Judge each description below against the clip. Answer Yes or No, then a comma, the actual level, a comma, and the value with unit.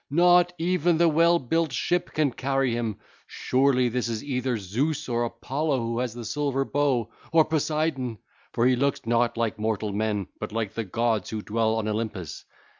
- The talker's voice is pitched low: Yes, low, 125 Hz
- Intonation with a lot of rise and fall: No, average, 4.7 semitones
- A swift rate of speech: No, average, 180 wpm